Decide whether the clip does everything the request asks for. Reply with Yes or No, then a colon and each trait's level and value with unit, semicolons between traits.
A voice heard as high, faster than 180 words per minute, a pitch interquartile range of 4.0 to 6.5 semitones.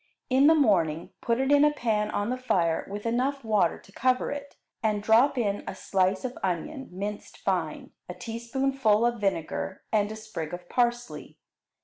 No: high, 220 Hz; average, 175 wpm; average, 4.7 semitones